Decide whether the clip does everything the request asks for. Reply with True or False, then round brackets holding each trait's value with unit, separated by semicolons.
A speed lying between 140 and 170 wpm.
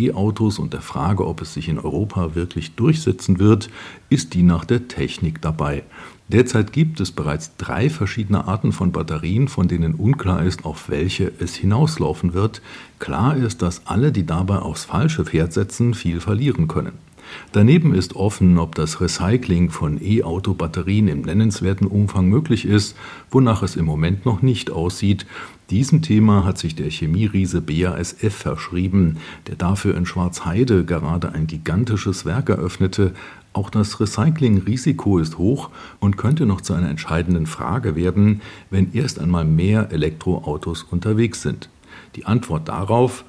True (150 wpm)